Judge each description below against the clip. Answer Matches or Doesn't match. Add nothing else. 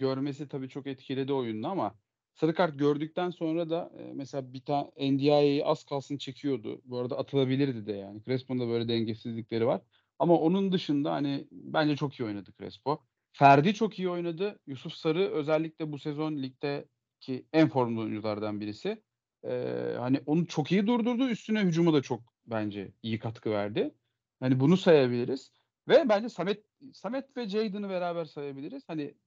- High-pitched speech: Doesn't match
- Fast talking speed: Matches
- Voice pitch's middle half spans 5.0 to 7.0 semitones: Matches